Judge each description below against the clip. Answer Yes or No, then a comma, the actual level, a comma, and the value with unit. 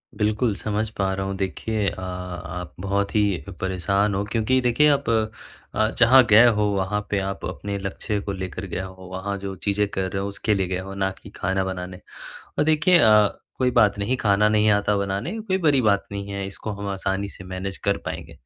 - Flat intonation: Yes, narrow, 1.9 semitones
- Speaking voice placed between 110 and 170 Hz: No, low, 100 Hz